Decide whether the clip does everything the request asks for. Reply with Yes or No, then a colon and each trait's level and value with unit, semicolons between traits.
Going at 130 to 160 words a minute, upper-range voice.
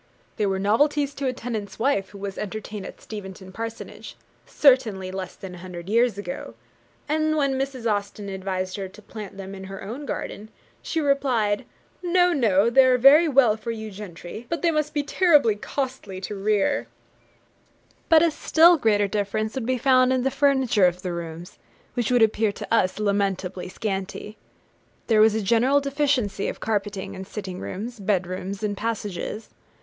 No: average, 175 wpm; high, 215 Hz